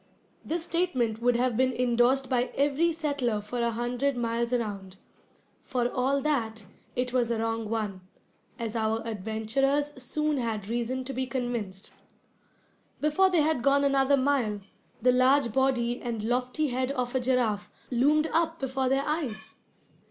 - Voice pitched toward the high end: Yes, very high, 250 Hz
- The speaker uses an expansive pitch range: No, average, 3.2 semitones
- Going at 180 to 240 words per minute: No, average, 150 wpm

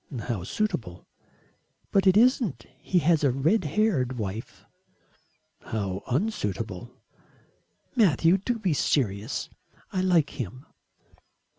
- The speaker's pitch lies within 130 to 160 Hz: Yes, medium, 140 Hz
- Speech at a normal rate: No, slow, 105 wpm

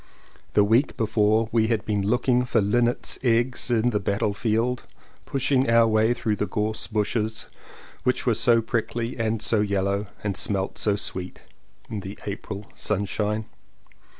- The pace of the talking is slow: No, average, 150 wpm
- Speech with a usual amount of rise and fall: No, narrow, 2.3 semitones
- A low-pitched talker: Yes, low, 110 Hz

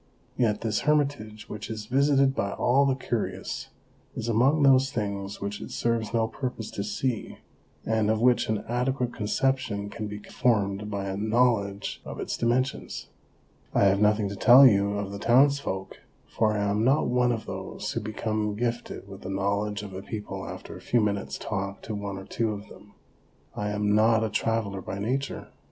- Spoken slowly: No, average, 185 wpm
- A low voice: Yes, low, 110 Hz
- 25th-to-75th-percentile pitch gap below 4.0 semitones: Yes, average, 3.1 semitones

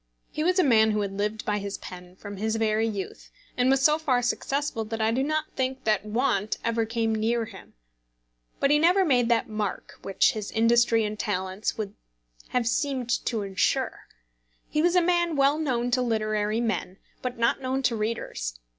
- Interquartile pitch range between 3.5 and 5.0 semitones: Yes, average, 3.8 semitones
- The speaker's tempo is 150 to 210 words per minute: Yes, average, 190 wpm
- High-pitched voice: Yes, high, 230 Hz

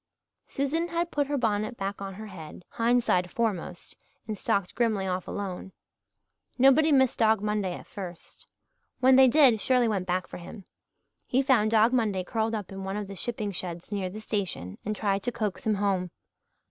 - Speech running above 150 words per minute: Yes, average, 185 wpm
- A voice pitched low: No, high, 210 Hz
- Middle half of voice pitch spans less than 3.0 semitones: No, average, 4.0 semitones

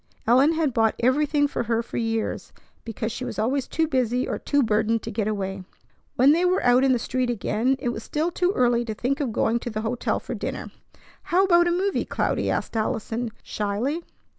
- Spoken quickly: Yes, fast, 210 wpm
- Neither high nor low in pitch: No, high, 245 Hz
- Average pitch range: Yes, average, 4.4 semitones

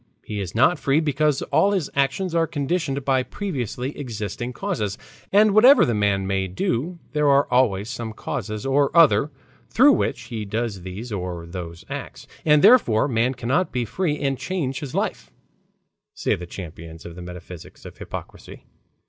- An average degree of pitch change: No, wide, 7.1 semitones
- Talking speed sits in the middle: Yes, average, 165 wpm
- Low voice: Yes, low, 130 Hz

